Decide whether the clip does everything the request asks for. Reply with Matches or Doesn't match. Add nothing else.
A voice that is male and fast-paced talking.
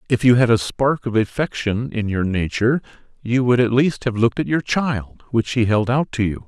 Matches